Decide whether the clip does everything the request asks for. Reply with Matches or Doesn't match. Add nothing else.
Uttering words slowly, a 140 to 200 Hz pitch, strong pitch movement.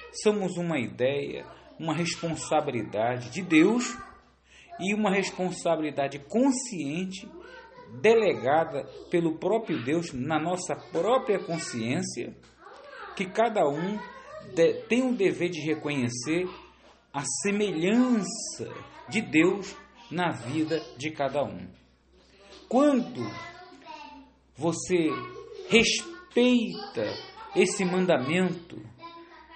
Matches